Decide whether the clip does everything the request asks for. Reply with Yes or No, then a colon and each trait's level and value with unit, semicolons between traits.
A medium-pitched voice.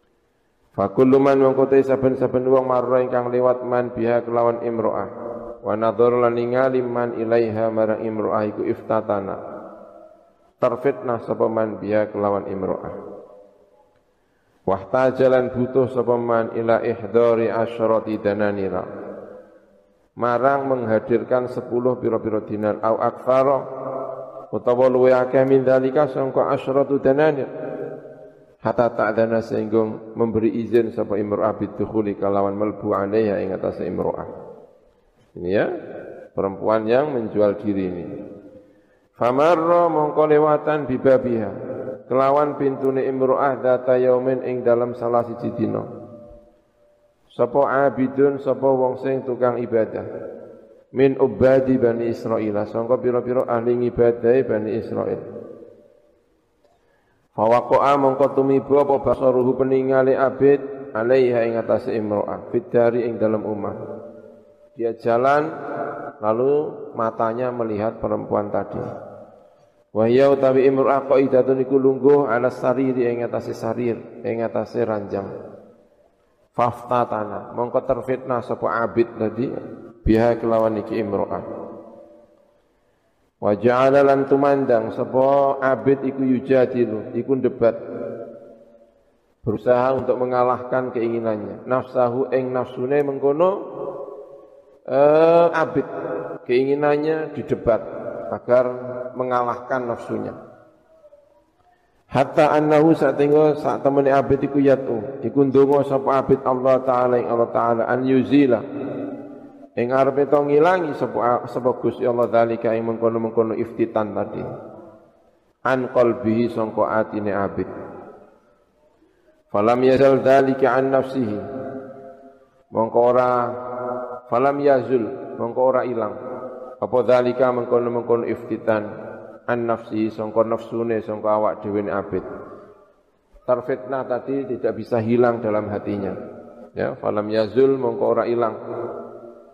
No: low, 125 Hz